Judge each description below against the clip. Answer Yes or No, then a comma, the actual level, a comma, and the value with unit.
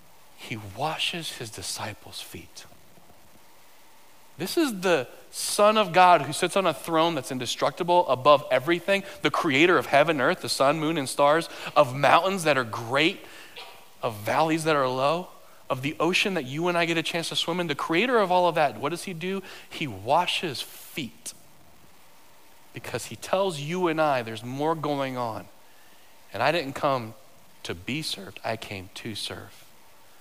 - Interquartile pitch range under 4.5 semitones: No, wide, 5.5 semitones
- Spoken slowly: No, average, 175 wpm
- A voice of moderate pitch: Yes, medium, 155 Hz